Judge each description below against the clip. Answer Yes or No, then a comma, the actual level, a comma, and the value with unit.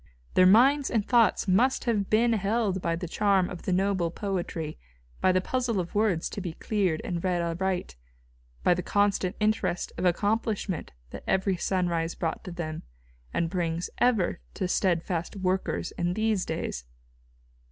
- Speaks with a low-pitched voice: No, medium, 185 Hz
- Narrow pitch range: No, average, 3.2 semitones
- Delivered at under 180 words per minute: Yes, average, 160 wpm